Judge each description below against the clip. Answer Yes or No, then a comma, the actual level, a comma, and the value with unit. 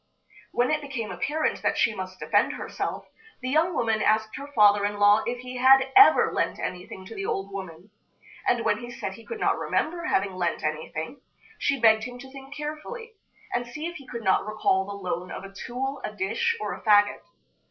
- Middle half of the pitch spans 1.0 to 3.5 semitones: No, wide, 5.4 semitones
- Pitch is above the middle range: Yes, high, 225 Hz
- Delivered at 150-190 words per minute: No, fast, 205 wpm